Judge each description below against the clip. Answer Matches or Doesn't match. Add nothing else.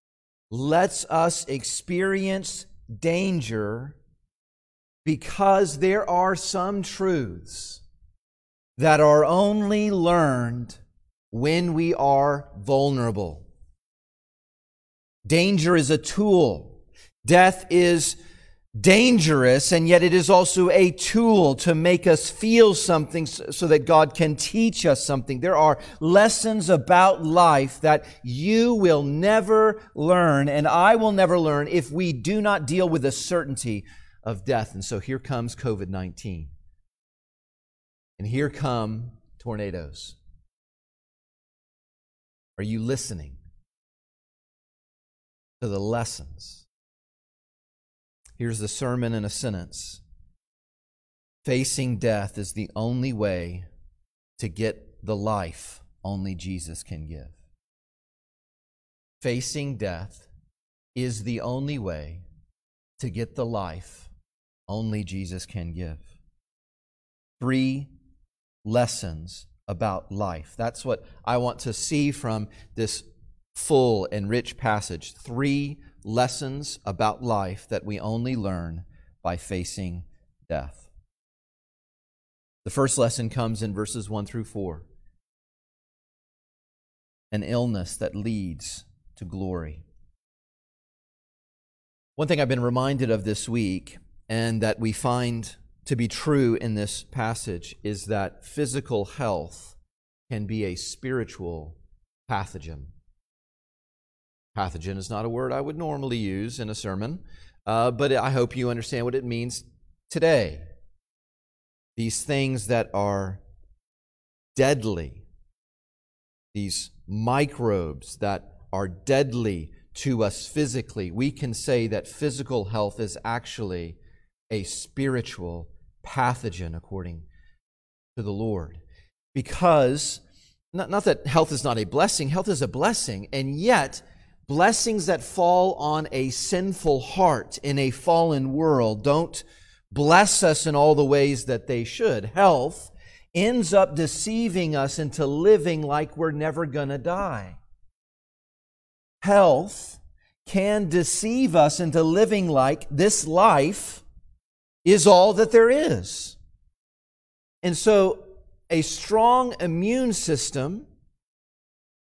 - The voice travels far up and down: Matches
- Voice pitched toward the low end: Matches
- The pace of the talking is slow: Matches